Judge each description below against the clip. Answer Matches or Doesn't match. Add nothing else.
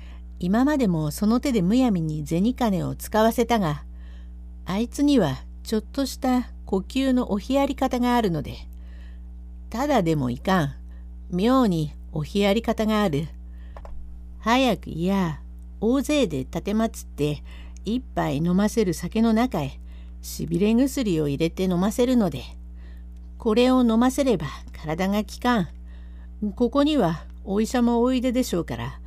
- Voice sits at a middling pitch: Matches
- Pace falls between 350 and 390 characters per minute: Doesn't match